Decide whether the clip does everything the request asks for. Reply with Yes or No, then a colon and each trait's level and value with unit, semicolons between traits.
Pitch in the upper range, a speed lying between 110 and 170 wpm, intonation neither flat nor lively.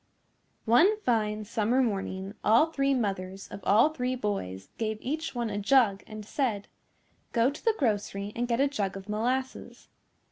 Yes: high, 225 Hz; average, 165 wpm; average, 4.3 semitones